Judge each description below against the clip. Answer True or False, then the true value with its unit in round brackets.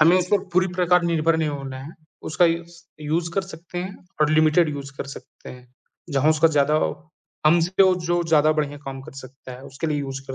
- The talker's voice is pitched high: False (155 Hz)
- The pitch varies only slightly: False (3.5 semitones)